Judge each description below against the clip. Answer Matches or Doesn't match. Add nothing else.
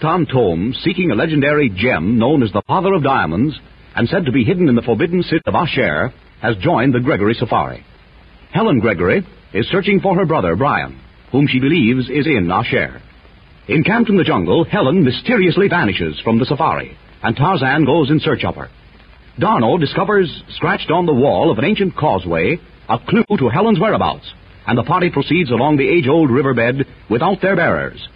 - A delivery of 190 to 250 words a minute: Doesn't match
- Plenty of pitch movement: Matches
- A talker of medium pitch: Matches